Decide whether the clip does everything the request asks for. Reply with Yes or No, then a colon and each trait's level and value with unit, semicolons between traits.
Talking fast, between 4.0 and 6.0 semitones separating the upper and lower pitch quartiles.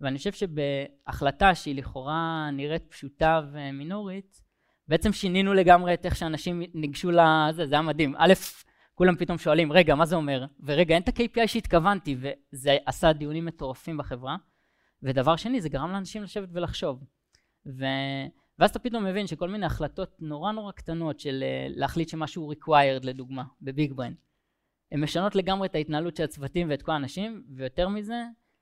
Yes: fast, 155 wpm; average, 4.7 semitones